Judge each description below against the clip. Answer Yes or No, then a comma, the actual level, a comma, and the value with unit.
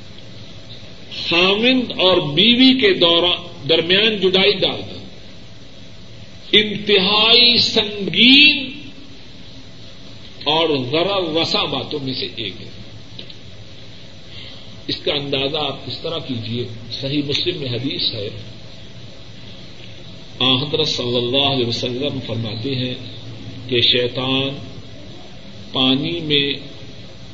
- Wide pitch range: Yes, wide, 6.6 semitones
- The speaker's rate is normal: No, slow, 90 wpm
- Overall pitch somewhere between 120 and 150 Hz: Yes, medium, 140 Hz